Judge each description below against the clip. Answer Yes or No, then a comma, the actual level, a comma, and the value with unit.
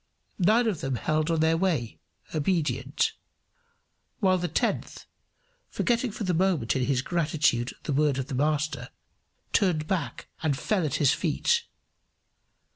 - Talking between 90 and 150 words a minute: Yes, average, 140 wpm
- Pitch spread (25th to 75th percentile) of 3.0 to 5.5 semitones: Yes, average, 4.8 semitones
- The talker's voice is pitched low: No, medium, 155 Hz